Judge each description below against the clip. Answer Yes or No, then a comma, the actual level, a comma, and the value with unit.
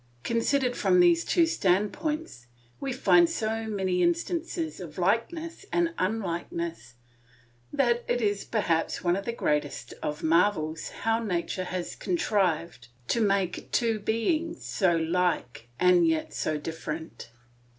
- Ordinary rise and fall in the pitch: No, wide, 5.8 semitones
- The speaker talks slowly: Yes, slow, 130 wpm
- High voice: Yes, high, 195 Hz